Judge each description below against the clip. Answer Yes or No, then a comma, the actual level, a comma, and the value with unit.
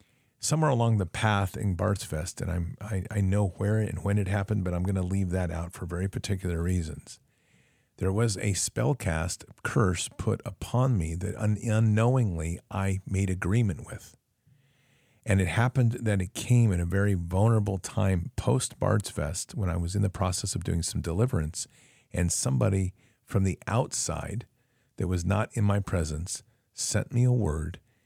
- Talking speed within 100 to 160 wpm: No, average, 175 wpm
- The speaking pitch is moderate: No, low, 105 Hz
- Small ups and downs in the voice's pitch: No, average, 4.2 semitones